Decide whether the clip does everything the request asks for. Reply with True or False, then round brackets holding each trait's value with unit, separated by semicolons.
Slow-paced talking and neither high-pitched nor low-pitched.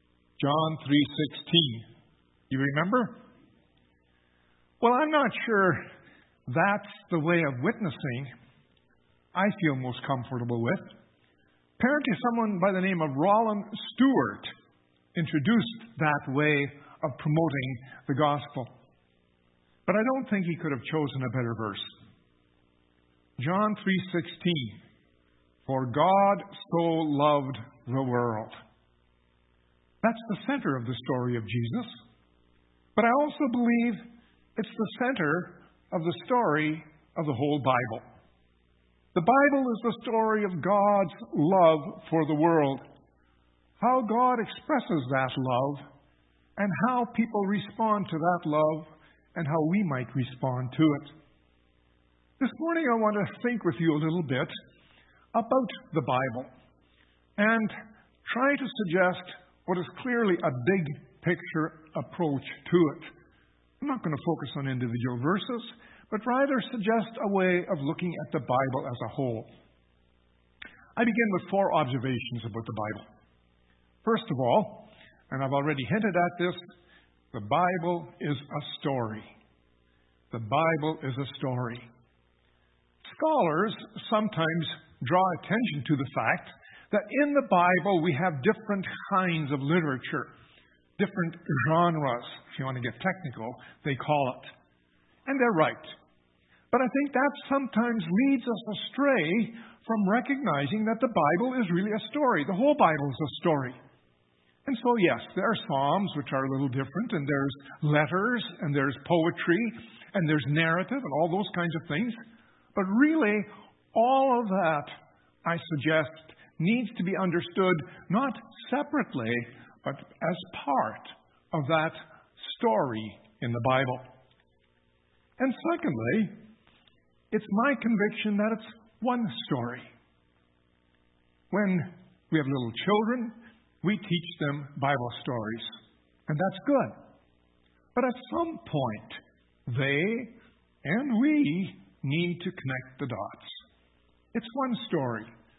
True (130 wpm; 160 Hz)